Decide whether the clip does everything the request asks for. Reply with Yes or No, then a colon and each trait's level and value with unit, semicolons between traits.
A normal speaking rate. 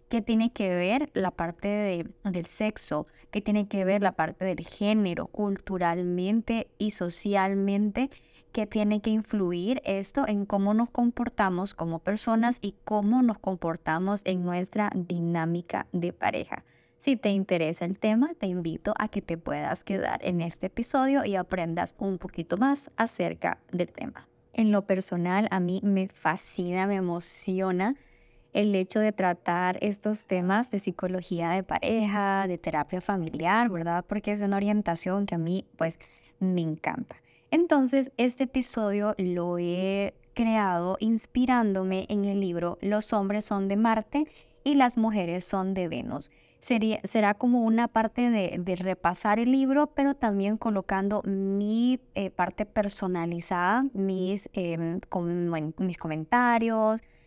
Yes: average, 145 wpm